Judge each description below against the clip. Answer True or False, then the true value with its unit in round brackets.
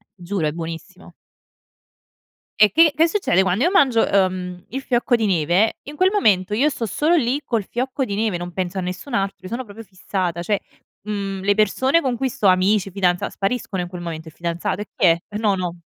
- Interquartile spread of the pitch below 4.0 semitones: False (4.9 semitones)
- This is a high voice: True (200 Hz)